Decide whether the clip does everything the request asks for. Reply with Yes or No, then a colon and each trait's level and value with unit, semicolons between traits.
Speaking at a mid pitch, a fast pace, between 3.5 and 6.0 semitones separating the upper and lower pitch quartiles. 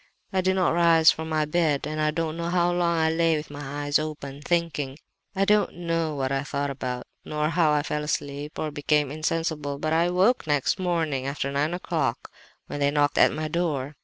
No: medium, 155 Hz; fast, 210 wpm; narrow, 2.6 semitones